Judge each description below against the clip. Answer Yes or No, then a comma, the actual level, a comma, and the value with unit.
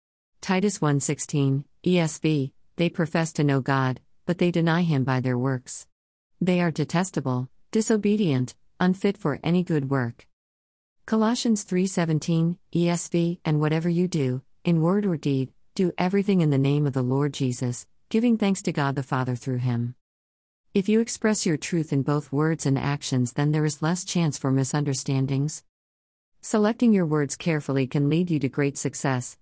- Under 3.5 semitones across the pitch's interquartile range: No, average, 4.8 semitones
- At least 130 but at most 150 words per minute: No, average, 160 wpm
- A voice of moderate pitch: Yes, medium, 150 Hz